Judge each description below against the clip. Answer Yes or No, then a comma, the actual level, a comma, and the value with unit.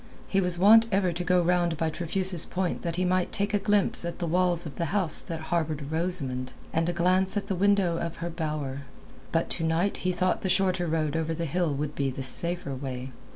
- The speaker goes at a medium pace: No, fast, 225 wpm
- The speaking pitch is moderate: Yes, medium, 170 Hz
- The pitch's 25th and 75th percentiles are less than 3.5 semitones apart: Yes, narrow, 2.6 semitones